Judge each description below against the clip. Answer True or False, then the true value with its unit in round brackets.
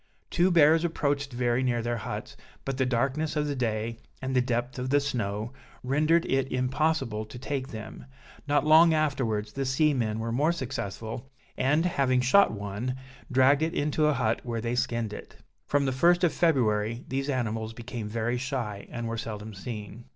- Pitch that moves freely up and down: False (3.9 semitones)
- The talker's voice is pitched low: True (125 Hz)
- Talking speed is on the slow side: False (180 wpm)